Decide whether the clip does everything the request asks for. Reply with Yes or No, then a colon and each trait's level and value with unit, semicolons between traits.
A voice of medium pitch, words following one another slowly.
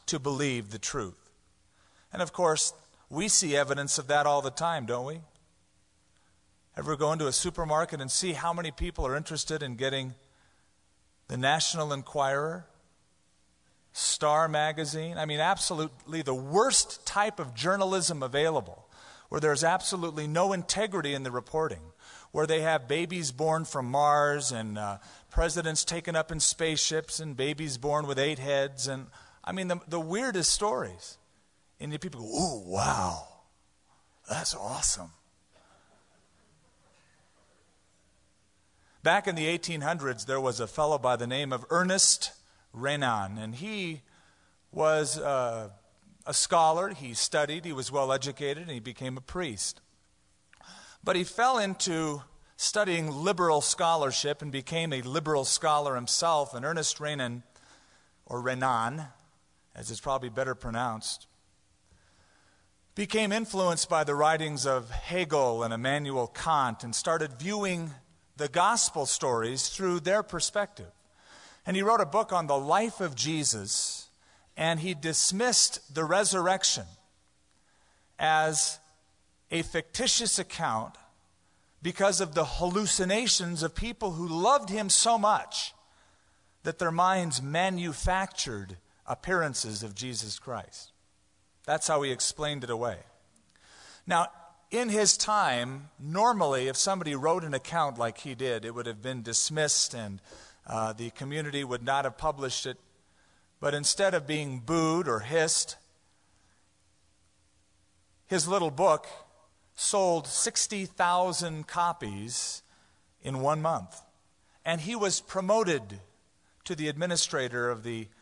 Yes: medium, 150 Hz; slow, 130 wpm